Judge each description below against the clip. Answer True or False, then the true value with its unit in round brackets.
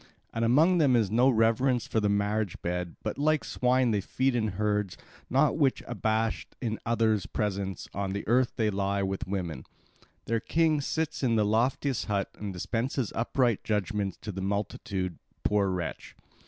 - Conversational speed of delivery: True (170 wpm)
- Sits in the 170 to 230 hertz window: False (110 Hz)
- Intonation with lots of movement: False (3.8 semitones)